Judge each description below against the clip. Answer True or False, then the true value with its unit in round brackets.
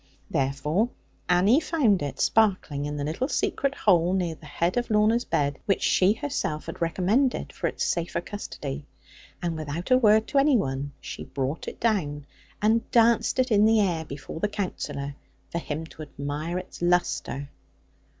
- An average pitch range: False (6.9 semitones)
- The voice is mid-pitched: True (180 Hz)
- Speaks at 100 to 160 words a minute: False (170 wpm)